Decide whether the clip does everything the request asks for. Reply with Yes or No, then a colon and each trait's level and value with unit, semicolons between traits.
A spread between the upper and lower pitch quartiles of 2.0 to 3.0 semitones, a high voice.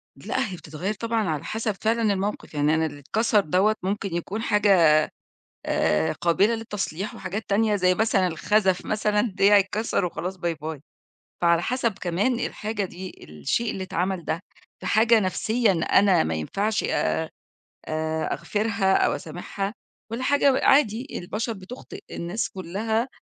No: average, 3.8 semitones; high, 200 Hz